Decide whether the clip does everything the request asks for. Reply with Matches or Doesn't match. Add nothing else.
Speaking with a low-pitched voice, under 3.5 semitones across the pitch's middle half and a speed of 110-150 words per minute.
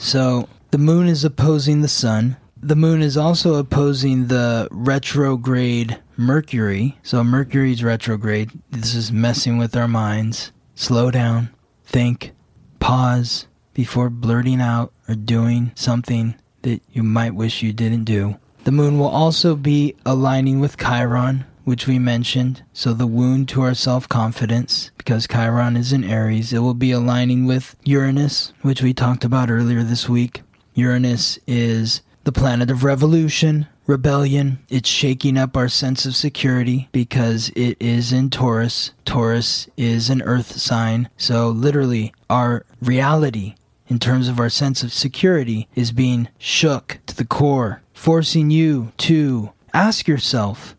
Matches